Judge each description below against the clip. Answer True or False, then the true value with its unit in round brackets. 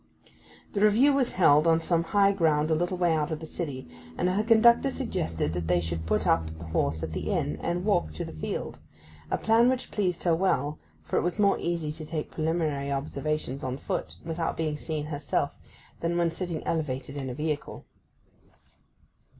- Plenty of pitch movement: False (4.4 semitones)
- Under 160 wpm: False (190 wpm)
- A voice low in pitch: False (160 Hz)